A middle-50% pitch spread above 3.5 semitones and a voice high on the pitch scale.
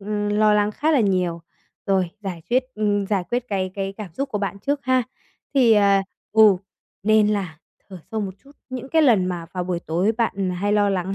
No: narrow, 2.6 semitones; high, 205 Hz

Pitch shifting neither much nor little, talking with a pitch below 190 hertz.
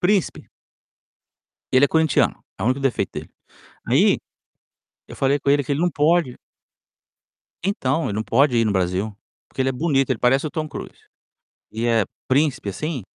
Yes: average, 4.4 semitones; low, 135 Hz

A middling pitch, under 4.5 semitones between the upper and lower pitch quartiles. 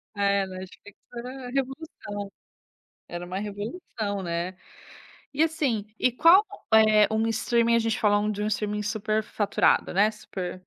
No: high, 215 Hz; average, 2.9 semitones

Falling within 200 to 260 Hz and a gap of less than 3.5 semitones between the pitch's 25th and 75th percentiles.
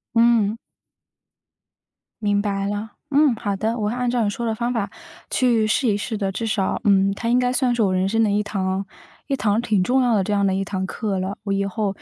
Yes: high, 210 Hz; average, 3.0 semitones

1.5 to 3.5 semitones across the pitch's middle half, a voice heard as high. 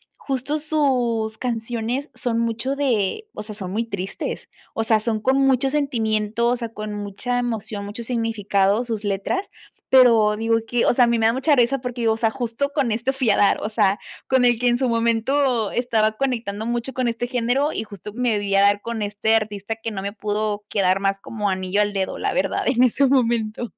Yes: average, 2.8 semitones; high, 230 Hz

